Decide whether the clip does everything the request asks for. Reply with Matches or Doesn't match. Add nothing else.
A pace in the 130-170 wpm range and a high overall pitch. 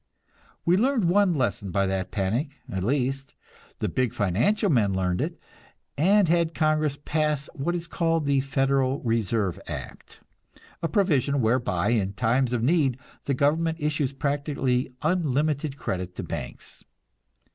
Doesn't match